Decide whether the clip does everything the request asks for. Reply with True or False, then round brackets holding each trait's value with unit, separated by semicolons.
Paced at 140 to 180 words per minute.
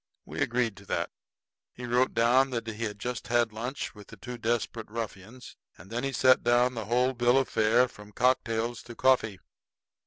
False (190 wpm)